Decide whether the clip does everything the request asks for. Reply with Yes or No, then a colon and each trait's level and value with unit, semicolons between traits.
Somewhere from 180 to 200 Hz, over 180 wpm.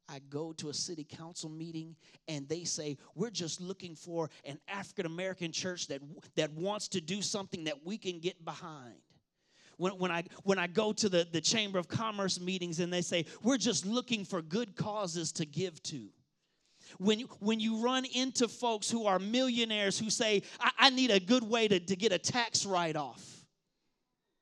Yes: medium, 185 Hz; average, 195 wpm